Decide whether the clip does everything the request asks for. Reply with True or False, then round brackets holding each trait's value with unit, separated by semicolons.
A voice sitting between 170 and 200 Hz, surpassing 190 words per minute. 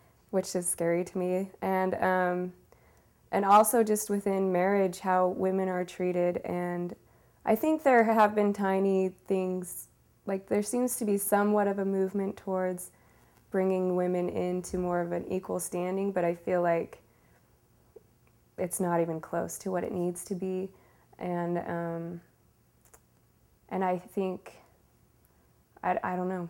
False (185 Hz; 145 wpm)